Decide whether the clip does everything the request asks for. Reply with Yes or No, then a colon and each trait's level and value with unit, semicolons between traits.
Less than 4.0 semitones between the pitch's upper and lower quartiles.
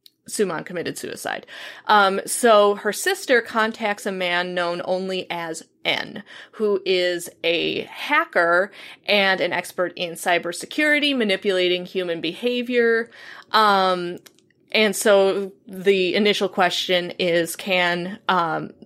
Yes: average, 3.3 semitones